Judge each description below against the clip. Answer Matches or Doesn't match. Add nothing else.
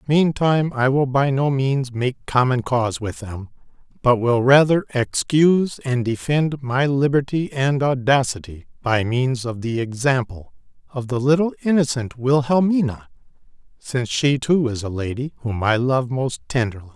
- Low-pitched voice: Matches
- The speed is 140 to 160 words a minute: Matches